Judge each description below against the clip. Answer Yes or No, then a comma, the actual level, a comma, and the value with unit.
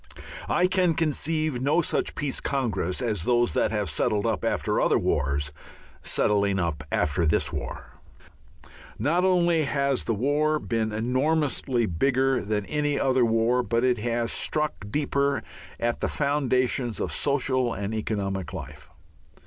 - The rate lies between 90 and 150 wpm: Yes, average, 140 wpm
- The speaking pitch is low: Yes, low, 125 Hz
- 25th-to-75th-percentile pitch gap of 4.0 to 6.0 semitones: Yes, average, 5.3 semitones